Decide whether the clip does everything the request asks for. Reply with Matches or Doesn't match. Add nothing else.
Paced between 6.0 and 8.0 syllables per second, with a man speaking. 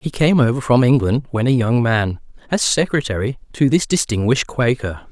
Doesn't match